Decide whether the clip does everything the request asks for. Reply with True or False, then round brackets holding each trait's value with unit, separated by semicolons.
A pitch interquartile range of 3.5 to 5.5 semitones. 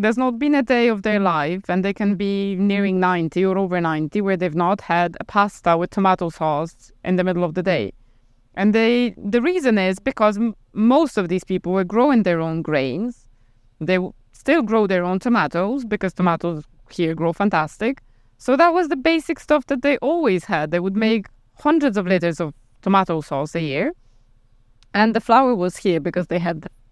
True (4.9 semitones)